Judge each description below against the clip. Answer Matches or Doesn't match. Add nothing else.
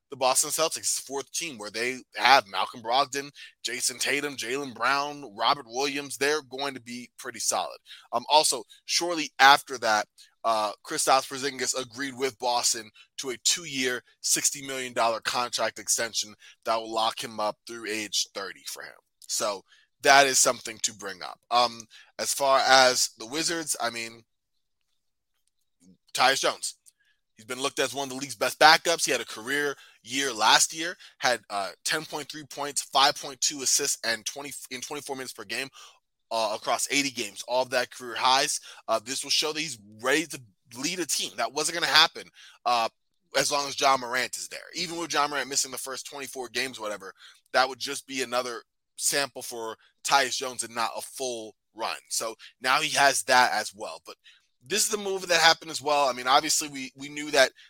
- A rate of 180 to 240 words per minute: Matches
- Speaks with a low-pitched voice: Matches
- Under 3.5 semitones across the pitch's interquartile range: Matches